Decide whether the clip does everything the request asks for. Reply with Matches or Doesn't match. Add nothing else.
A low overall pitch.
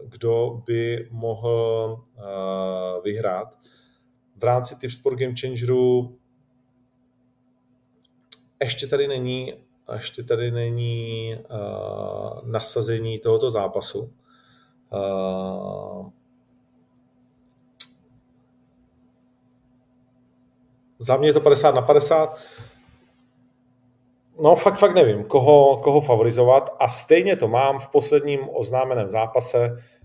Matches